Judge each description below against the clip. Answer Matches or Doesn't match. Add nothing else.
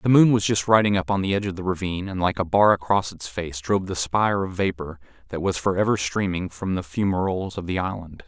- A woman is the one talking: Doesn't match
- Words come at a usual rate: Doesn't match